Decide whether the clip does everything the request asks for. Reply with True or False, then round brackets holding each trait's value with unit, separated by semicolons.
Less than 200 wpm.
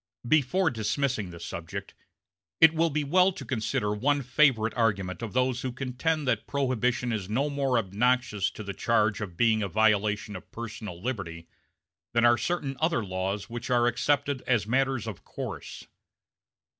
True (160 wpm)